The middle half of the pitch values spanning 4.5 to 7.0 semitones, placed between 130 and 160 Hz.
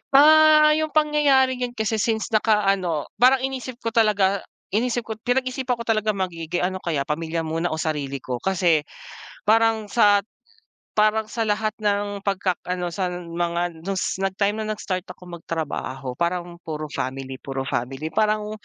No: average, 5.0 semitones; high, 200 Hz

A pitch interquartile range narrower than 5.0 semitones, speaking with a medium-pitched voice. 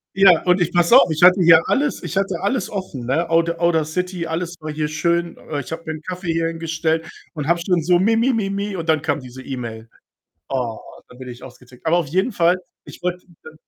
Yes: average, 2.7 semitones; medium, 165 Hz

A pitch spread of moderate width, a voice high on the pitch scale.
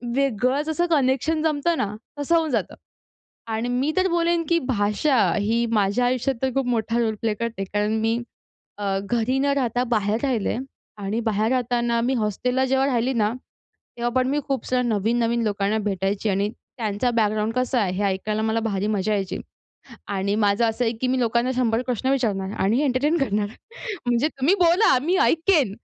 Yes: average, 3.8 semitones; high, 235 Hz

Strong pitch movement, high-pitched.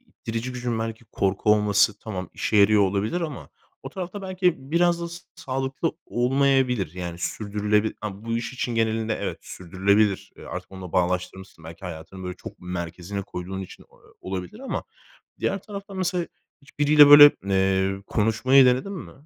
No: wide, 6.3 semitones; low, 110 Hz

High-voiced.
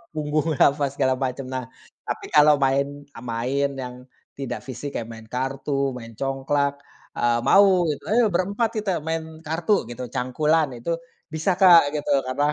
No: medium, 140 Hz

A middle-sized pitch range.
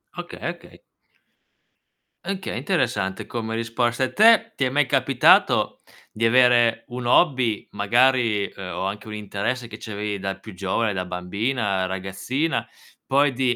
Yes: average, 4.2 semitones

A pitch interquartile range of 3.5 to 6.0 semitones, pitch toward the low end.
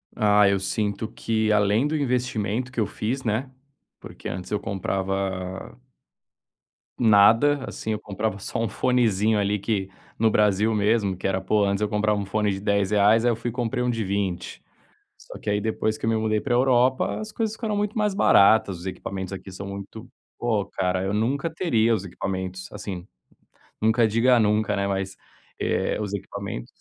No: average, 2.9 semitones; low, 105 Hz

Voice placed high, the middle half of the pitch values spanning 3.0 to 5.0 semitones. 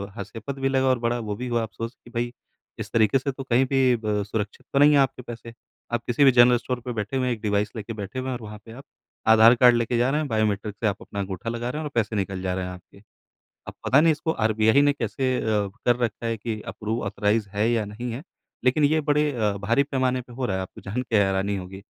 No: low, 115 Hz; average, 3.5 semitones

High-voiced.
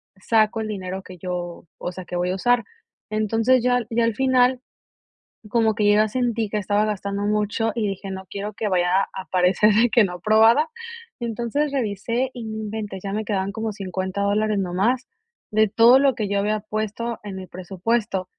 Yes: high, 210 Hz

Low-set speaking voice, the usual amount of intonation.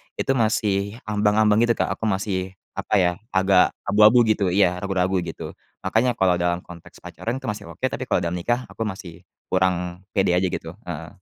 Yes: very low, 95 Hz; average, 3.0 semitones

